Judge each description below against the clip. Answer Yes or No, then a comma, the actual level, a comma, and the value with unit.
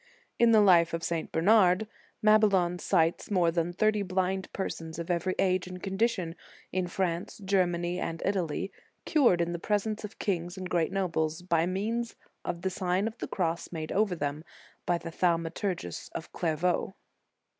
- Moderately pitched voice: Yes, medium, 180 Hz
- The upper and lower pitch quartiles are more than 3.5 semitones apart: No, narrow, 2.6 semitones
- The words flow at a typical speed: Yes, average, 165 wpm